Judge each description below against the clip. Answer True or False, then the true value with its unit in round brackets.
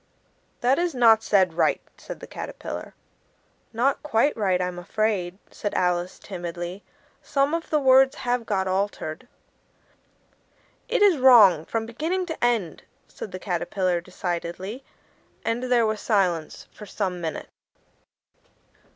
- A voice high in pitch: True (210 Hz)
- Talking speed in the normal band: False (130 wpm)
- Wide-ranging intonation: True (5.9 semitones)